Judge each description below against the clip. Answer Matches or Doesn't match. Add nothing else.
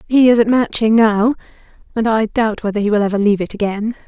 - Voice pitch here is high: Matches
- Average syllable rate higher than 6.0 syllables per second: Matches